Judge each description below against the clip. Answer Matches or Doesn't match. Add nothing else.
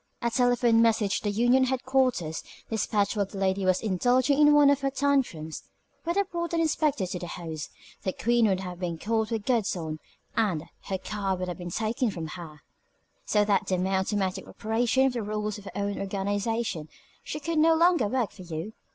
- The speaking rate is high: Matches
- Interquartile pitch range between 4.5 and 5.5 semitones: Matches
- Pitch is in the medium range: Doesn't match